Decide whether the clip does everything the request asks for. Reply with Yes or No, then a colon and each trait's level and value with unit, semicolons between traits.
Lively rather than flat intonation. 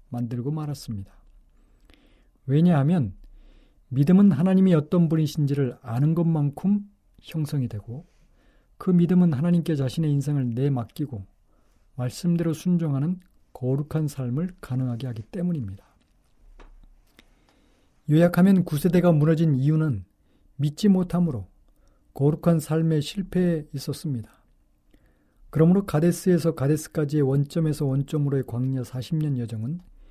No: average, 5.0 semitones